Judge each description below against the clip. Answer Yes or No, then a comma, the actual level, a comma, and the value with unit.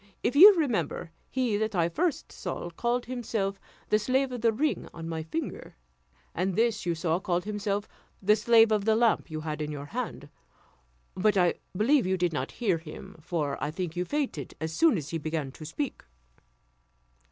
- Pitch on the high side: Yes, high, 195 Hz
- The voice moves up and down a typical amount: No, wide, 6.2 semitones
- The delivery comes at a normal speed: Yes, average, 185 wpm